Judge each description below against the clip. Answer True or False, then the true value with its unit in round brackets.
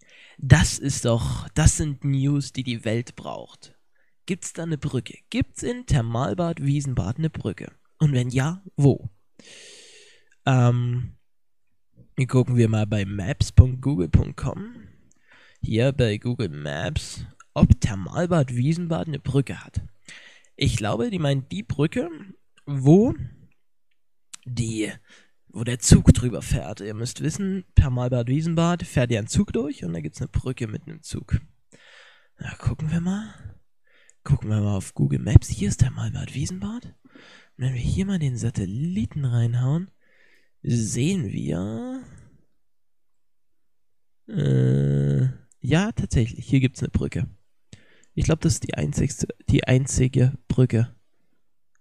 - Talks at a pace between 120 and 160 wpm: True (130 wpm)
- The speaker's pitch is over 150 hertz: False (130 Hz)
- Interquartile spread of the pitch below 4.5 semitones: False (5.3 semitones)